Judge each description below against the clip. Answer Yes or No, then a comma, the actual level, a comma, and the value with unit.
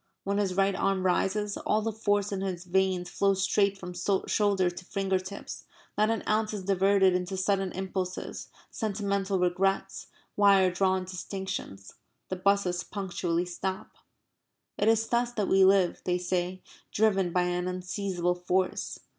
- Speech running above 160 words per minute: No, average, 150 wpm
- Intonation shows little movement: Yes, narrow, 1.6 semitones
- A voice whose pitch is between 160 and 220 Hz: Yes, high, 190 Hz